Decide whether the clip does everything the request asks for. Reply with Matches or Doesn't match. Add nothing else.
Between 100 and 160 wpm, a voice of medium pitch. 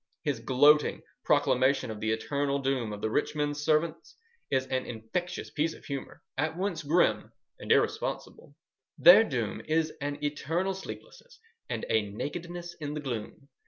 Matches